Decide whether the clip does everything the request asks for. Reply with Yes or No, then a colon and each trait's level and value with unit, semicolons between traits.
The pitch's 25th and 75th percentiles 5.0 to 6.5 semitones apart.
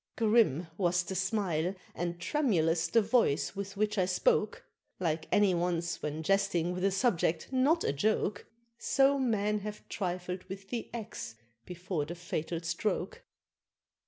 No: average, 3.6 semitones